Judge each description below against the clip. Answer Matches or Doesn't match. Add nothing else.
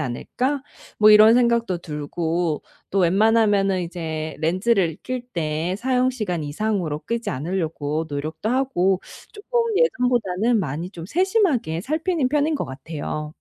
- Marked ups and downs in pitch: Matches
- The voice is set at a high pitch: Matches